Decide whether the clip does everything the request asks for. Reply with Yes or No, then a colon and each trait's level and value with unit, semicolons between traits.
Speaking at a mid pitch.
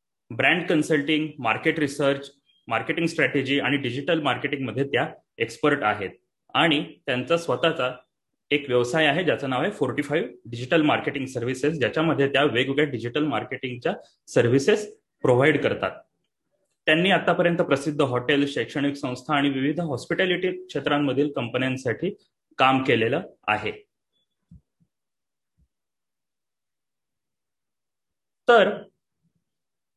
Yes: medium, 145 Hz